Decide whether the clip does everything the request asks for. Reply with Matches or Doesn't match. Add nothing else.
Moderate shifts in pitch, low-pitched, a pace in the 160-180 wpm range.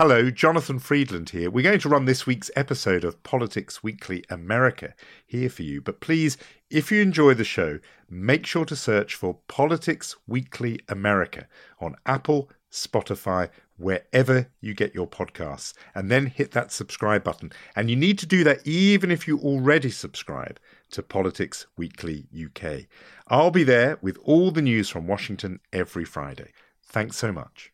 Doesn't match